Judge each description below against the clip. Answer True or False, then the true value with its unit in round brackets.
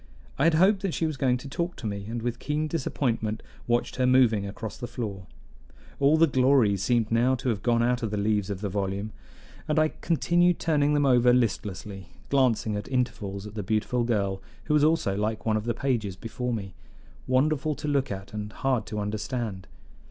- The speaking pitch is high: False (120 Hz)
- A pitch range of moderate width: True (4.8 semitones)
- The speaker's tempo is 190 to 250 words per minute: True (205 wpm)